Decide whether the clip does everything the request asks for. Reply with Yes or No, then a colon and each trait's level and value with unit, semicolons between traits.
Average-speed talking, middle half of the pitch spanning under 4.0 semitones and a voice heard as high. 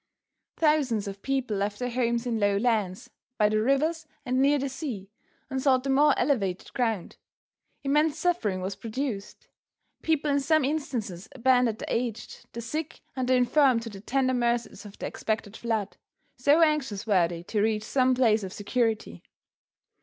No: average, 170 wpm; average, 4.5 semitones; high, 240 Hz